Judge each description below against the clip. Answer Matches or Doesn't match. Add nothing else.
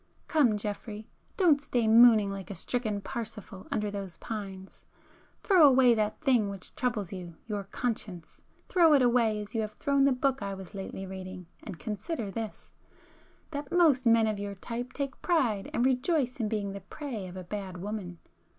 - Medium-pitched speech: Doesn't match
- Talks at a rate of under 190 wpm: Matches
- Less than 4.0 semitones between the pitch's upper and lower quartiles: Doesn't match